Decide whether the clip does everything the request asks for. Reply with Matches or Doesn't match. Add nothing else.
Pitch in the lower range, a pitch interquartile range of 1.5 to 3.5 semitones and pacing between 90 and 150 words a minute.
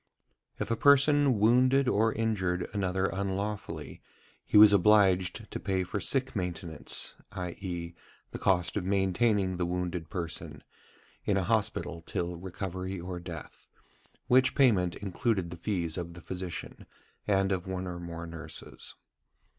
Matches